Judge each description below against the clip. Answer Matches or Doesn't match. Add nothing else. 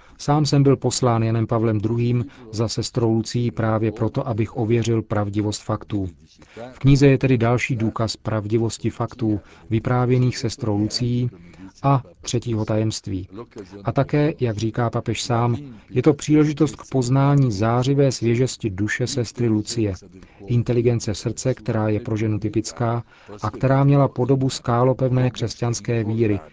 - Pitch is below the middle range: Matches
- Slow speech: Doesn't match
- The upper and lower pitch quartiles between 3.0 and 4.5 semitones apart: Doesn't match